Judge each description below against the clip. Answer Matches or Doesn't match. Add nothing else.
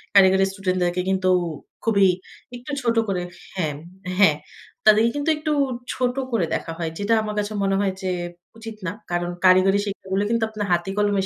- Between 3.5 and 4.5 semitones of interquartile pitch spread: Doesn't match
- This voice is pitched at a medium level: Doesn't match